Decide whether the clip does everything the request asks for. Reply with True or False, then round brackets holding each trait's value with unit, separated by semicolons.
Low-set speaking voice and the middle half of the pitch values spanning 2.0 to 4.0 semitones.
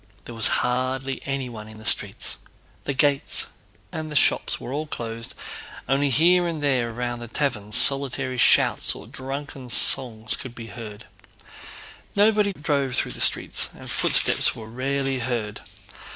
True (130 Hz; 3.2 semitones)